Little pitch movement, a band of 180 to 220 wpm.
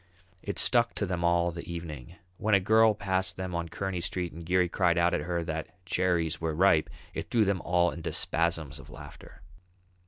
Yes: narrow, 2.0 semitones; average, 195 wpm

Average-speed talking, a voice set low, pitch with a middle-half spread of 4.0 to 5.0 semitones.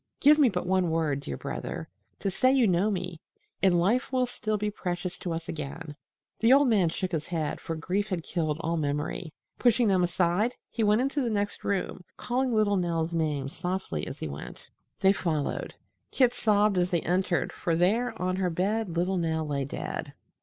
No: average, 195 wpm; medium, 180 Hz; average, 4.4 semitones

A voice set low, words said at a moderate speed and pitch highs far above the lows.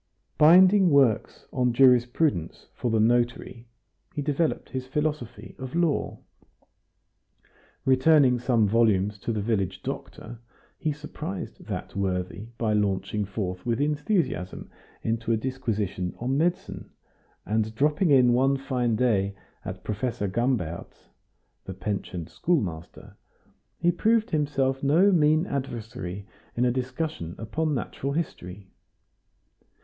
No: low, 125 Hz; slow, 115 wpm; wide, 5.8 semitones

